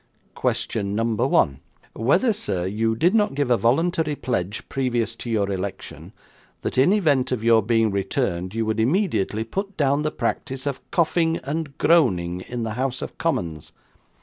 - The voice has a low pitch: Yes, low, 120 Hz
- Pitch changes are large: Yes, wide, 5.8 semitones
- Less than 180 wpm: Yes, average, 165 wpm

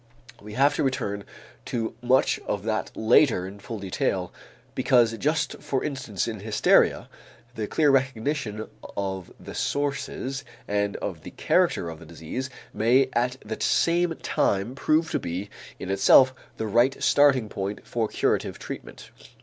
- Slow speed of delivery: No, average, 150 wpm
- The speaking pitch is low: Yes, low, 115 Hz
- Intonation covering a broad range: No, average, 4.8 semitones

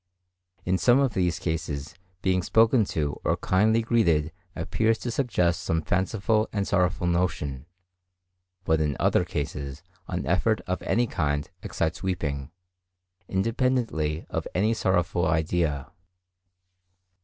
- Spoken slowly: Yes, slow, 125 wpm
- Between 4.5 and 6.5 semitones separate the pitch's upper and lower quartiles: Yes, wide, 5.6 semitones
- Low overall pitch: Yes, very low, 90 Hz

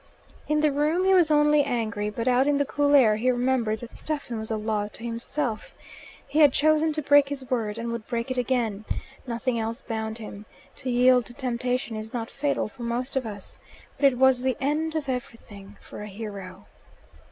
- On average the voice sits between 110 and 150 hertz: No, high, 245 Hz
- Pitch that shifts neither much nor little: Yes, average, 4.2 semitones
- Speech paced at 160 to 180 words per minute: No, fast, 205 wpm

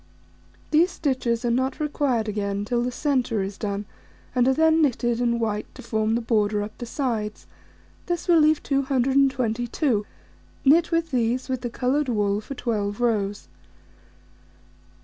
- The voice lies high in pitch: Yes, high, 240 Hz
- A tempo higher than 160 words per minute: No, average, 150 wpm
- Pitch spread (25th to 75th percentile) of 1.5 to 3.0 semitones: No, average, 4.2 semitones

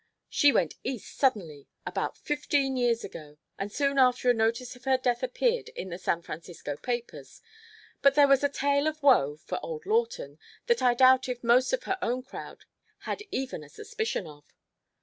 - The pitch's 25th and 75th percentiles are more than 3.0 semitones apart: Yes, average, 4.3 semitones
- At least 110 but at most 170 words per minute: No, average, 185 wpm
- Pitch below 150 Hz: No, very high, 255 Hz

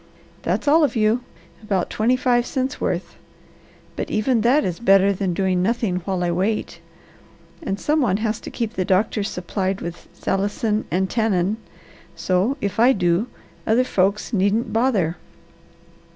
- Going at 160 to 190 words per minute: No, average, 150 wpm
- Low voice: No, high, 210 Hz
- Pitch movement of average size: Yes, average, 4.0 semitones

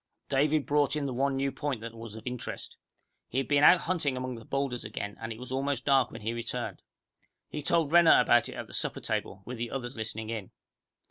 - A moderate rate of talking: No, fast, 225 wpm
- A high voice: No, low, 130 Hz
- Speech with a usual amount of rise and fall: Yes, average, 3.7 semitones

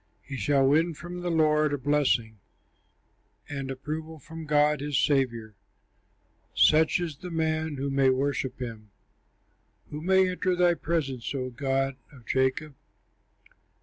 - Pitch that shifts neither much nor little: Yes, average, 3.0 semitones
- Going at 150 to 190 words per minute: No, slow, 135 wpm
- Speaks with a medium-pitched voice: Yes, medium, 145 Hz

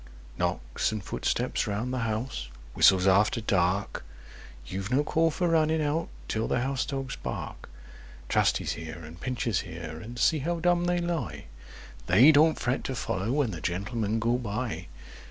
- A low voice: Yes, low, 115 Hz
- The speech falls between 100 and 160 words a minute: Yes, average, 155 wpm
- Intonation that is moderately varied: No, wide, 7.3 semitones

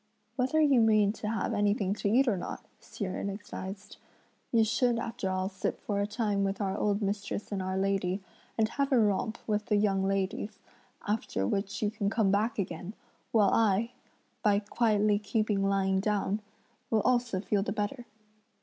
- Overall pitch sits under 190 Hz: No, high, 205 Hz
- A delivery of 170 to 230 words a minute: Yes, average, 175 wpm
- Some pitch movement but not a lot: No, narrow, 2.0 semitones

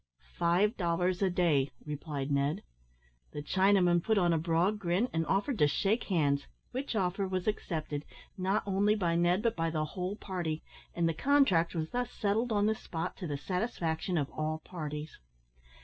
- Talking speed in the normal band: Yes, average, 175 wpm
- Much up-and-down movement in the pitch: No, average, 4.0 semitones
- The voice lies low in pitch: No, medium, 175 Hz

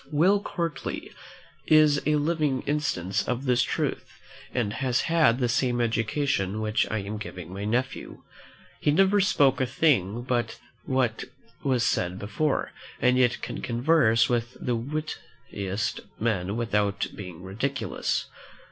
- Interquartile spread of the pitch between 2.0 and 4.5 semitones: No, average, 5.3 semitones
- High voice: No, low, 125 Hz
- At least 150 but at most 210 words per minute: No, slow, 135 wpm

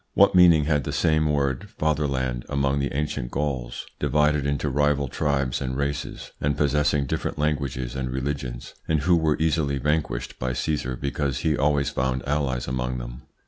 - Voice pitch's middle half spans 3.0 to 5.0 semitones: No, narrow, 2.4 semitones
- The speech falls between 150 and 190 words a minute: Yes, average, 165 wpm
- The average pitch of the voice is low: Yes, very low, 70 Hz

